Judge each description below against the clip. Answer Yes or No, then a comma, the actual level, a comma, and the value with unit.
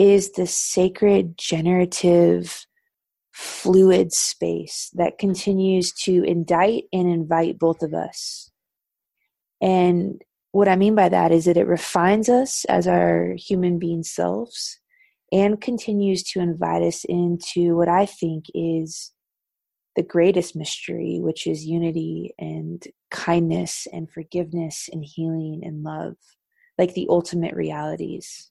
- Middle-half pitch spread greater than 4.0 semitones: No, narrow, 2.5 semitones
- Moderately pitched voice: Yes, medium, 175 Hz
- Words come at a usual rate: No, slow, 125 wpm